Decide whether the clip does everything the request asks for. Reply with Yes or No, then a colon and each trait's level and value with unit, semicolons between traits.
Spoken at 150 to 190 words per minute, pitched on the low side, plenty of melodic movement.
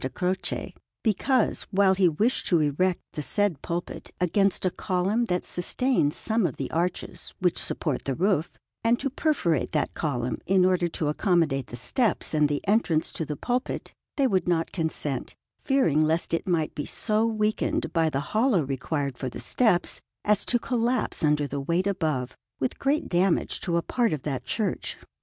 No: average, 175 wpm; medium, 175 Hz; wide, 5.9 semitones